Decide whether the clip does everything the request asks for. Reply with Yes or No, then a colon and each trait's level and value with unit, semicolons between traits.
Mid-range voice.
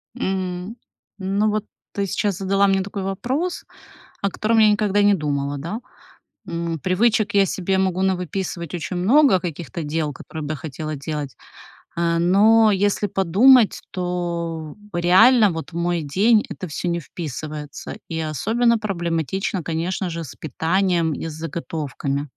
Yes: medium, 180 Hz